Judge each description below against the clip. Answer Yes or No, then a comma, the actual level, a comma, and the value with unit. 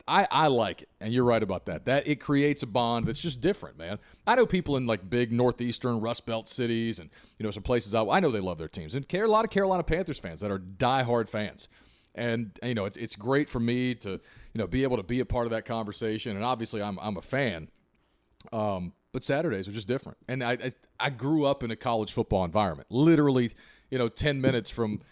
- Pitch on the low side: Yes, low, 120 Hz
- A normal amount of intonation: Yes, average, 3.5 semitones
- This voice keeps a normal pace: No, fast, 245 wpm